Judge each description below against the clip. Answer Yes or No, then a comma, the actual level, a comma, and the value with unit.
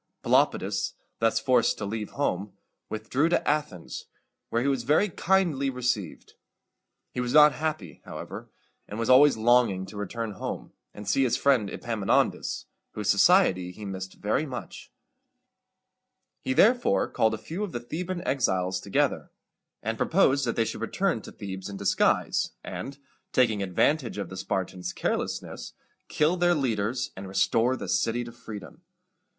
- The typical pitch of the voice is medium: No, low, 115 Hz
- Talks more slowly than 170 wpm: Yes, average, 150 wpm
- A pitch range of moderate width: No, wide, 5.7 semitones